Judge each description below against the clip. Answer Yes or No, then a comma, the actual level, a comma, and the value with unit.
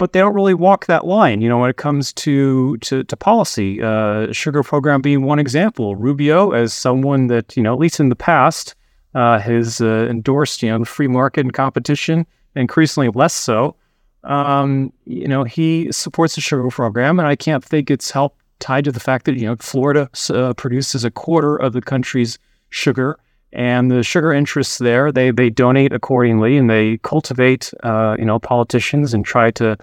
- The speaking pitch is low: Yes, low, 130 Hz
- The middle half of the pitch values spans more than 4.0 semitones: No, average, 3.6 semitones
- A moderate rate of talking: Yes, average, 195 wpm